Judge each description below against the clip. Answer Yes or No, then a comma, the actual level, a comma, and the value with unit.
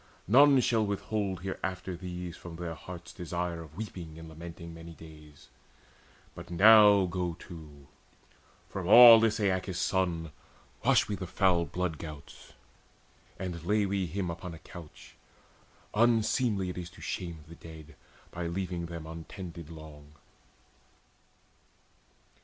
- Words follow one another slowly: Yes, slow, 130 wpm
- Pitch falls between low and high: No, very low, 90 Hz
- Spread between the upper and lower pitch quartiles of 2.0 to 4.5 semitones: Yes, average, 2.8 semitones